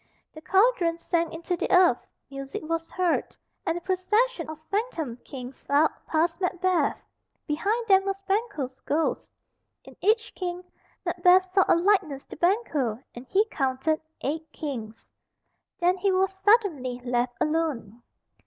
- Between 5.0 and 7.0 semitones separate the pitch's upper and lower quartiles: Yes, average, 5.3 semitones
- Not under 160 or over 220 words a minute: No, average, 140 wpm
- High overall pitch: Yes, very high, 335 Hz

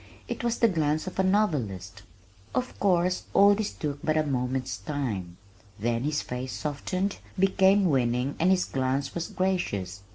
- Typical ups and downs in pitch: No, wide, 7.0 semitones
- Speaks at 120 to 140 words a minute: No, average, 160 wpm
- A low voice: No, medium, 150 Hz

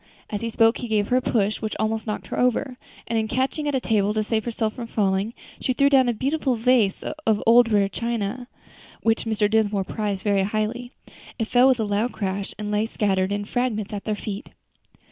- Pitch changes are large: No, average, 2.8 semitones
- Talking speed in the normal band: No, fast, 215 wpm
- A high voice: Yes, high, 220 Hz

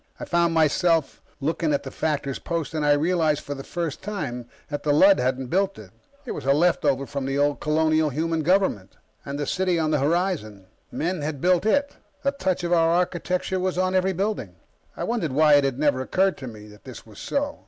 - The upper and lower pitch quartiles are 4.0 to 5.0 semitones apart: Yes, average, 4.6 semitones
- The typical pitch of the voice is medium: Yes, medium, 155 Hz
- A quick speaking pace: Yes, fast, 215 wpm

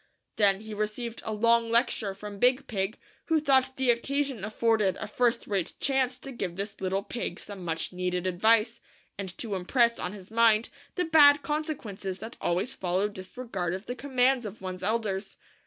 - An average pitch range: Yes, average, 4.4 semitones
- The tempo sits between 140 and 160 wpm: No, average, 185 wpm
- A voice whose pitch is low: No, high, 220 Hz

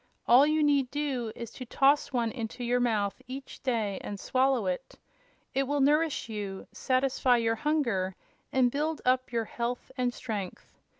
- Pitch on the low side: No, very high, 250 Hz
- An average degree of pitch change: Yes, average, 3.2 semitones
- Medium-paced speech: Yes, average, 165 wpm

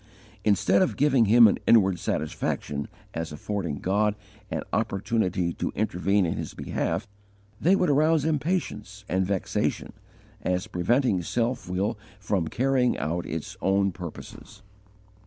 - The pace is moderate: No, slow, 130 wpm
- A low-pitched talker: Yes, low, 100 Hz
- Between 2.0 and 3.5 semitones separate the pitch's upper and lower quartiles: No, average, 4.8 semitones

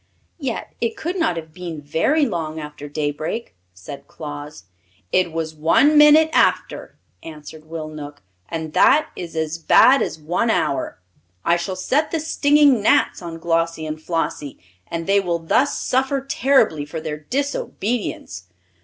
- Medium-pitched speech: Yes, medium, 165 Hz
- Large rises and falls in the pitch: Yes, wide, 8.4 semitones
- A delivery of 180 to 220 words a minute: No, average, 150 wpm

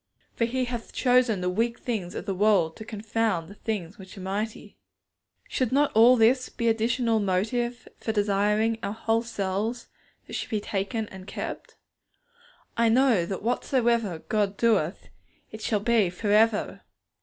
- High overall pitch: Yes, high, 220 Hz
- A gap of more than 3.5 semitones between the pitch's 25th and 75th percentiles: No, average, 2.7 semitones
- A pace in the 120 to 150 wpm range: No, average, 160 wpm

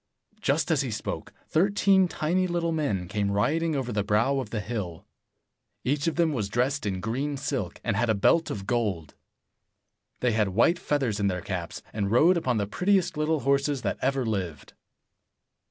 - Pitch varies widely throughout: Yes, wide, 7.0 semitones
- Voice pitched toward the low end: Yes, low, 125 Hz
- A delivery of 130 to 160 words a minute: No, average, 180 wpm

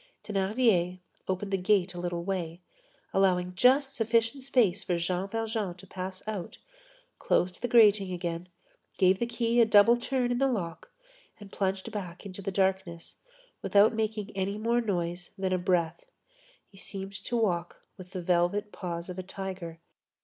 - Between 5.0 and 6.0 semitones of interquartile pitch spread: No, average, 3.4 semitones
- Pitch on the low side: No, high, 195 Hz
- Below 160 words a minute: No, average, 165 wpm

